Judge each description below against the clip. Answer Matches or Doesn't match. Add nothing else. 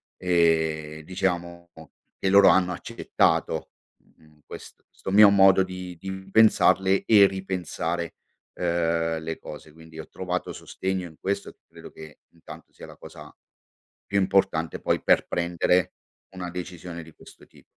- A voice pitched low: Matches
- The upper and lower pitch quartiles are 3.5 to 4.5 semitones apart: Doesn't match